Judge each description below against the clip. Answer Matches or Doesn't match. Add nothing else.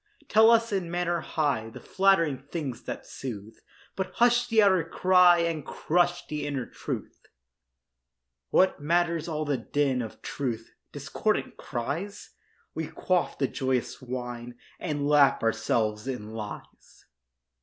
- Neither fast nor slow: Doesn't match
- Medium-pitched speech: Matches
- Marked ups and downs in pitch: Matches